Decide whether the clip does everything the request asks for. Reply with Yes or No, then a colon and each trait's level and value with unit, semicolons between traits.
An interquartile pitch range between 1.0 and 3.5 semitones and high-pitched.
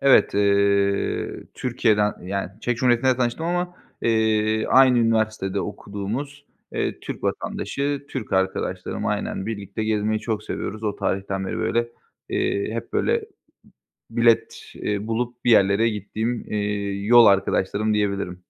No: average, 3.1 semitones; low, 110 Hz